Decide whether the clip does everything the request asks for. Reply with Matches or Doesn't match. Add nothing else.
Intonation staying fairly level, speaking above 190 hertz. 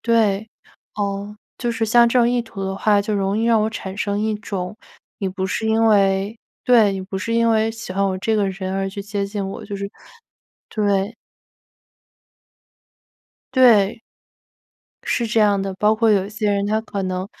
Matches